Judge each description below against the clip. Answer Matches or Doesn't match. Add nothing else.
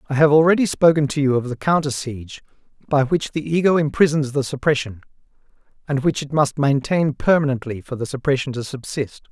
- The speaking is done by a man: Matches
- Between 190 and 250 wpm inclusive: Doesn't match